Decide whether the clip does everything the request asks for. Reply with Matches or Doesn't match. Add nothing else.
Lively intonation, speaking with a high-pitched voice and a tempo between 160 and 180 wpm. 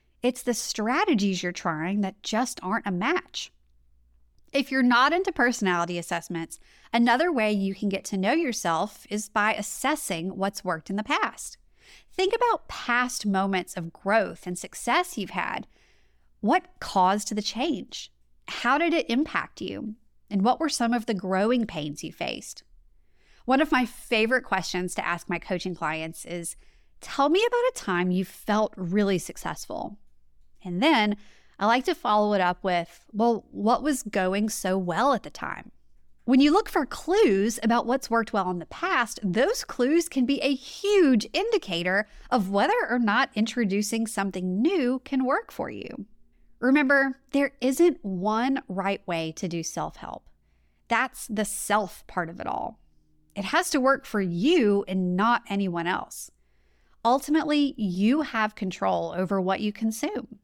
Matches